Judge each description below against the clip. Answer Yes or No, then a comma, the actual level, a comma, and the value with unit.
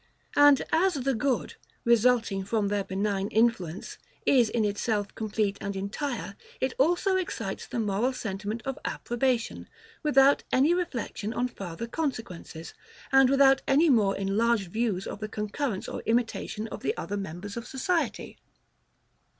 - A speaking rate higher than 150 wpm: No, average, 140 wpm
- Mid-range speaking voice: No, high, 230 Hz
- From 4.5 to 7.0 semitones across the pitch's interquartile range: Yes, average, 4.9 semitones